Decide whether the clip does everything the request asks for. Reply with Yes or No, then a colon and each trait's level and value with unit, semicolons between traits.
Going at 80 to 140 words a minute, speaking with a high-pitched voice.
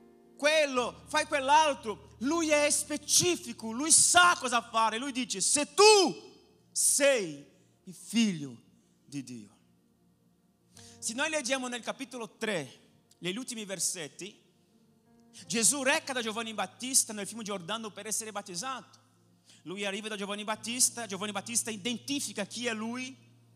Yes: average, 125 wpm; high, 225 Hz